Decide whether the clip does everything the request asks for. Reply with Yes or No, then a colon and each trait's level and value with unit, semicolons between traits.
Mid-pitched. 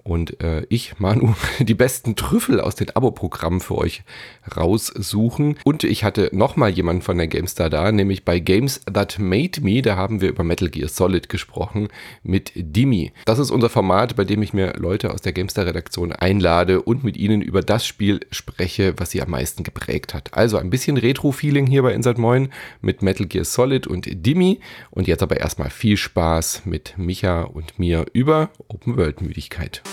No: low, 100 Hz